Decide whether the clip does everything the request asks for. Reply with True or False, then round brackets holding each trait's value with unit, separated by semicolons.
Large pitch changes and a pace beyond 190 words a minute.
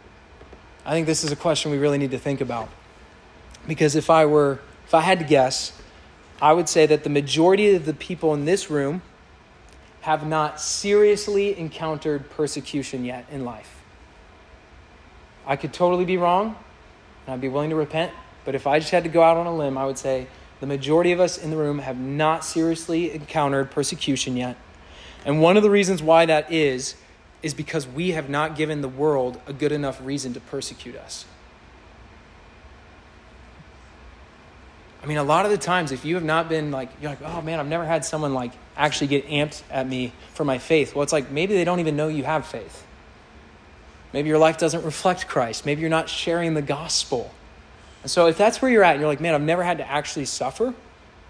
False (3.7 semitones; 200 wpm)